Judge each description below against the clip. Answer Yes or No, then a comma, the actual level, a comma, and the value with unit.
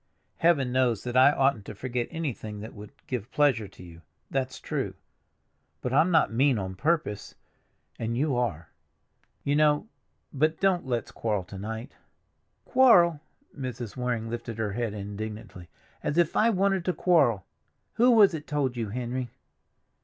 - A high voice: No, low, 125 Hz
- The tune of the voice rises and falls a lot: Yes, wide, 5.8 semitones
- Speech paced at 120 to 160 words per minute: Yes, average, 150 wpm